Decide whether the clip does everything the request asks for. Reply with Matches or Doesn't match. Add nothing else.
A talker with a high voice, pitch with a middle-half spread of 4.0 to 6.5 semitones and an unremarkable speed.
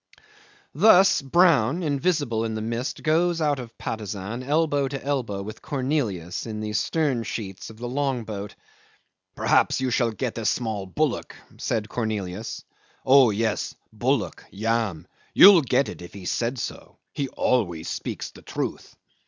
Doesn't match